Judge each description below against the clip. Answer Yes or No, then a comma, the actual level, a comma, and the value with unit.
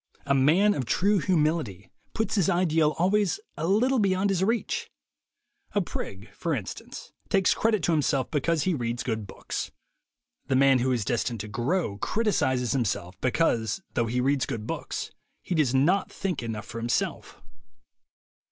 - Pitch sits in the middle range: Yes, medium, 145 Hz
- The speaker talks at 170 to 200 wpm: No, average, 160 wpm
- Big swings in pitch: Yes, wide, 7.8 semitones